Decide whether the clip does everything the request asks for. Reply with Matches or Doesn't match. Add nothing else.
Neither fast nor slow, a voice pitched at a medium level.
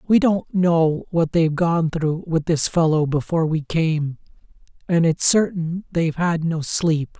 Matches